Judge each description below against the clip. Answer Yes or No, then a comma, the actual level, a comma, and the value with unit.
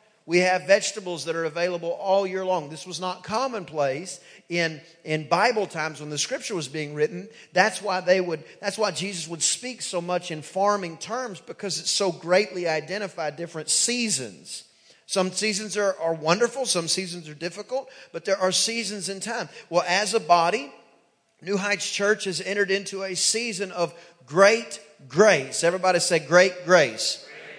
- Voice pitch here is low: No, medium, 185 Hz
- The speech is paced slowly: No, average, 170 wpm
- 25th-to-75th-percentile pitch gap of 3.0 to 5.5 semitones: Yes, average, 3.3 semitones